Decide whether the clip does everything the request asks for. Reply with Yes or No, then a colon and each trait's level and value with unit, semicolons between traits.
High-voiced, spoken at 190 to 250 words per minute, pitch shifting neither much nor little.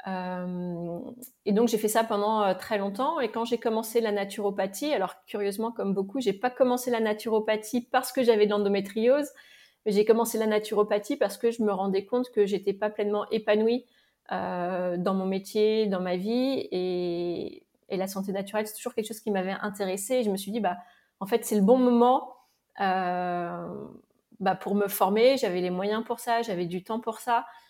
Yes: high, 215 Hz; average, 195 wpm; average, 3.3 semitones